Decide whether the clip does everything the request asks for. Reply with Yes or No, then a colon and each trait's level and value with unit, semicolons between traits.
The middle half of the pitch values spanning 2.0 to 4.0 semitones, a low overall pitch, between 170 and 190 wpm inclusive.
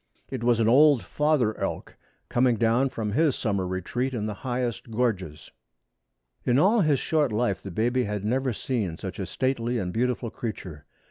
Yes: average, 3.7 semitones; low, 120 Hz; average, 175 wpm